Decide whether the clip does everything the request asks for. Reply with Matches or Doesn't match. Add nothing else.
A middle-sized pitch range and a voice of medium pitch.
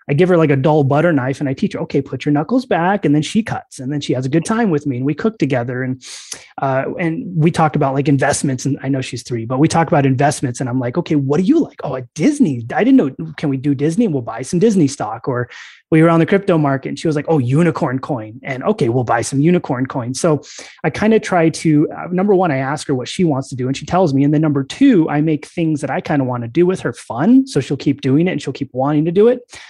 Matches